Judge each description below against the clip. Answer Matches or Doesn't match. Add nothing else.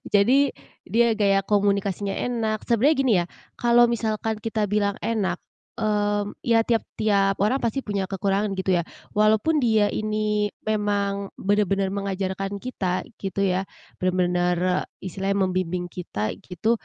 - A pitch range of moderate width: Doesn't match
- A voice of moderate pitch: Doesn't match